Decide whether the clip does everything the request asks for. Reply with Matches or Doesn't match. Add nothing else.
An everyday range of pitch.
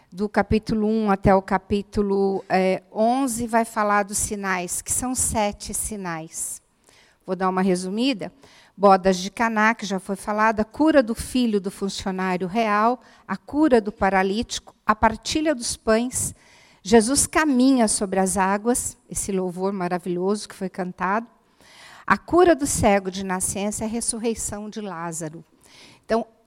Matches